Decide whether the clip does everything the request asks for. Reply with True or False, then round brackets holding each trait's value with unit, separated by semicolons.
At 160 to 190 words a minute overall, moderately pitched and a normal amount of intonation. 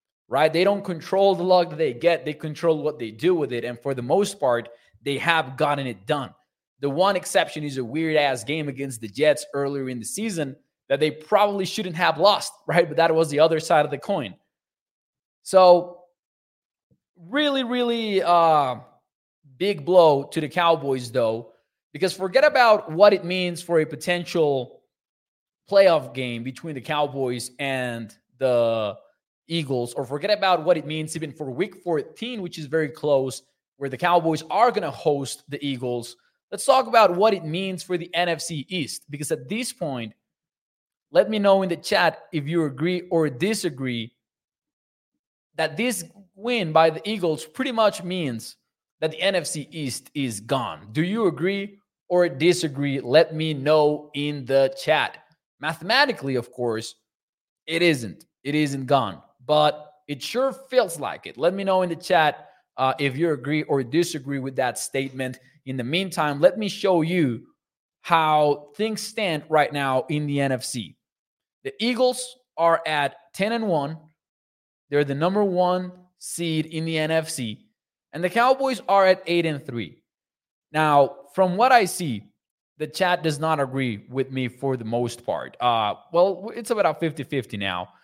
True (170 wpm; 160 Hz; 4.6 semitones)